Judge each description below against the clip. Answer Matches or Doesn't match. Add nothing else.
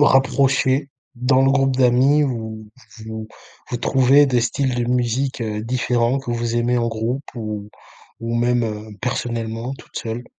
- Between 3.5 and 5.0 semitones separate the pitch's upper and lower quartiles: Doesn't match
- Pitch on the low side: Matches